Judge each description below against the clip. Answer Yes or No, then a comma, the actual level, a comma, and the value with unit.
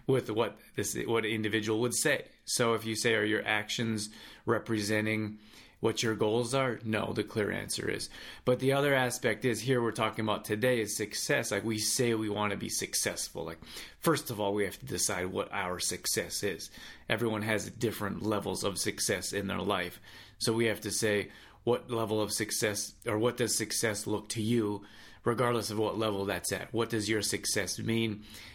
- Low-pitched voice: Yes, low, 110 Hz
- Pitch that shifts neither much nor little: No, narrow, 1.8 semitones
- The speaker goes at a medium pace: Yes, average, 195 wpm